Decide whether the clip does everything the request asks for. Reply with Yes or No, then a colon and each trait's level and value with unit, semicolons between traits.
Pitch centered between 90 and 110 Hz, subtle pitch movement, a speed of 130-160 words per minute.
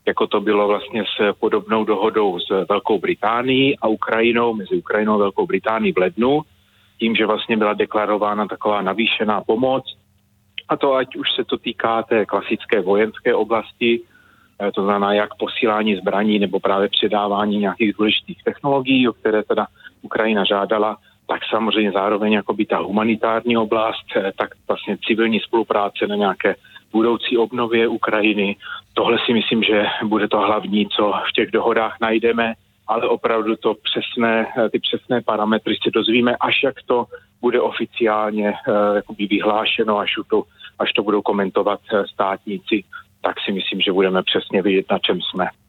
Yes: low, 105 Hz; narrow, 1.8 semitones; average, 150 wpm